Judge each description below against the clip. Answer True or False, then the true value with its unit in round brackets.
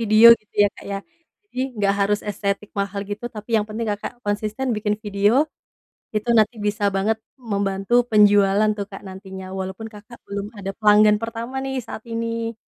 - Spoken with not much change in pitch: True (1.8 semitones)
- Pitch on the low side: False (210 Hz)